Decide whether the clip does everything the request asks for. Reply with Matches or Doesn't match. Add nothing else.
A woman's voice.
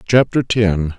Doesn't match